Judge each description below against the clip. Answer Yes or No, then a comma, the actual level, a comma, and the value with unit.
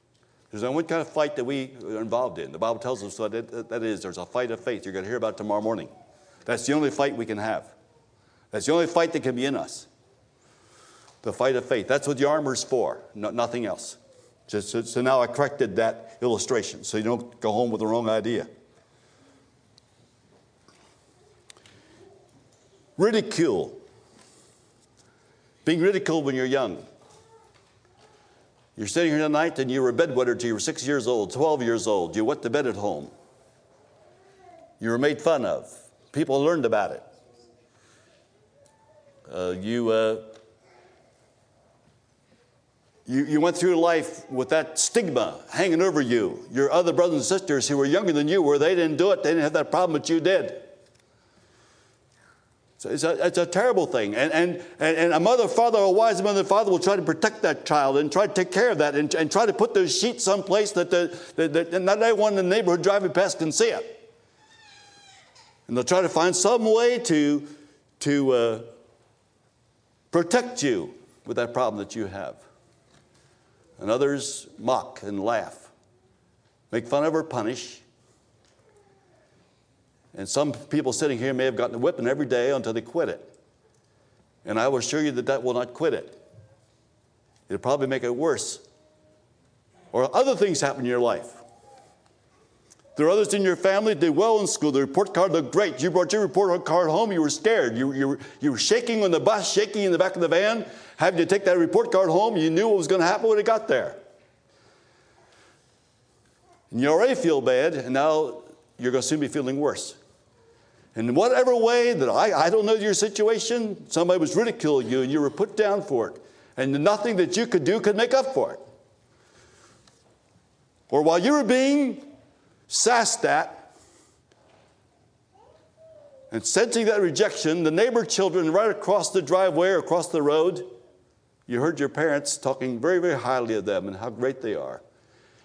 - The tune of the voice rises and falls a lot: Yes, wide, 8.2 semitones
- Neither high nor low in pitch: Yes, medium, 155 Hz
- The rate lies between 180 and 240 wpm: Yes, average, 185 wpm